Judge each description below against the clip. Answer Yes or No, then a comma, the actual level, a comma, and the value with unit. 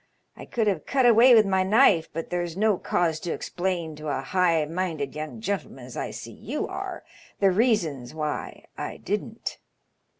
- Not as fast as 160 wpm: No, average, 175 wpm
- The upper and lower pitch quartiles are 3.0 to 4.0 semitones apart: No, average, 4.8 semitones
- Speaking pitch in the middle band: Yes, medium, 175 Hz